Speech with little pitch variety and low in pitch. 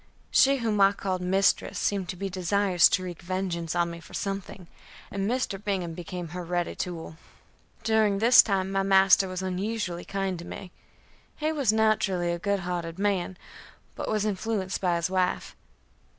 No: narrow, 2.3 semitones; high, 190 Hz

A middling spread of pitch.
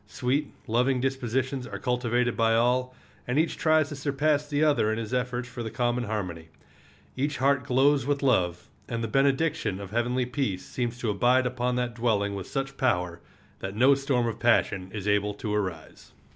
Yes: average, 3.8 semitones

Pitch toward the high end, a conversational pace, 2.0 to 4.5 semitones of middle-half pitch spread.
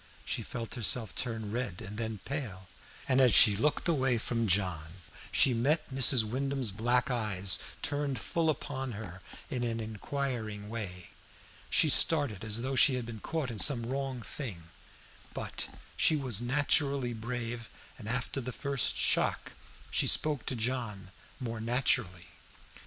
No: low, 120 Hz; average, 150 wpm; average, 3.7 semitones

